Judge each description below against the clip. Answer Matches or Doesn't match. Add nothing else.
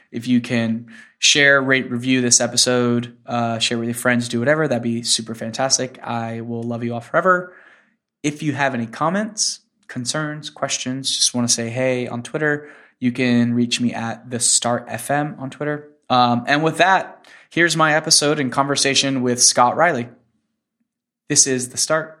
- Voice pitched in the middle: Doesn't match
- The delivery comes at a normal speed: Matches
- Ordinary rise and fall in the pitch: Matches